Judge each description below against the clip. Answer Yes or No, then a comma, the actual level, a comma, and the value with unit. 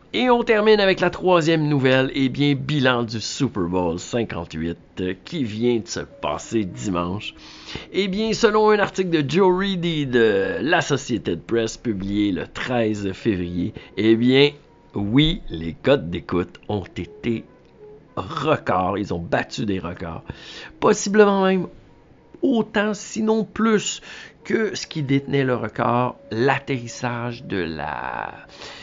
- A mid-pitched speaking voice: No, low, 125 Hz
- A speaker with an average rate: No, slow, 135 wpm